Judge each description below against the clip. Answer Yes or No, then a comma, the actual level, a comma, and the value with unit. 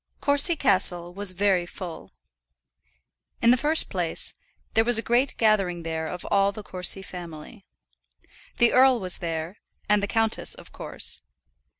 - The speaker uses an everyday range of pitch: Yes, average, 4.8 semitones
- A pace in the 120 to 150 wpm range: Yes, average, 145 wpm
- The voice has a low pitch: No, high, 200 Hz